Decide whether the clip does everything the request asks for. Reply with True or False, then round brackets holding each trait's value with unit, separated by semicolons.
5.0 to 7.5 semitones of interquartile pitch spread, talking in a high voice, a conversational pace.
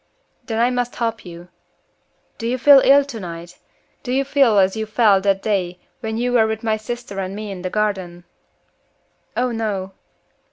False (4.0 semitones; 220 Hz; 175 wpm)